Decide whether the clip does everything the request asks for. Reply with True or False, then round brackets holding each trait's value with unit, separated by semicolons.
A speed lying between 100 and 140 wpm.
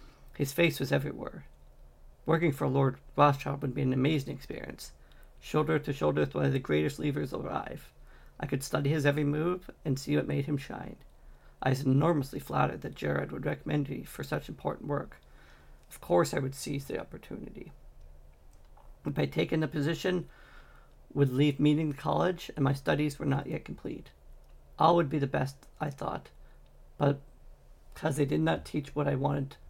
False (180 wpm)